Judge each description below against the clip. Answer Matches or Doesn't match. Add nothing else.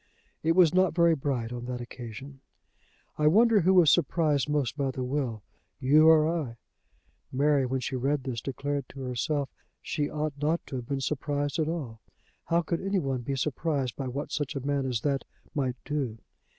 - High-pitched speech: Doesn't match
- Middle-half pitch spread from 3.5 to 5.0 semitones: Doesn't match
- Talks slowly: Doesn't match